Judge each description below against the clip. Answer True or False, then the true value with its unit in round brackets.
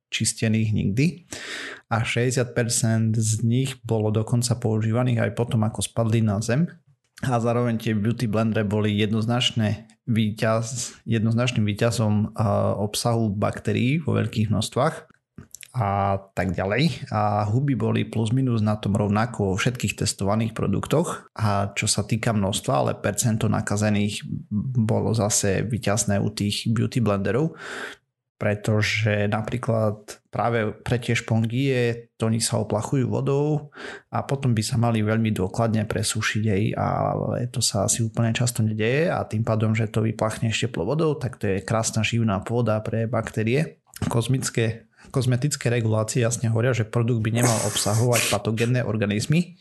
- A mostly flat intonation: True (2.1 semitones)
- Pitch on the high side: False (115 Hz)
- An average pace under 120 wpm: False (140 wpm)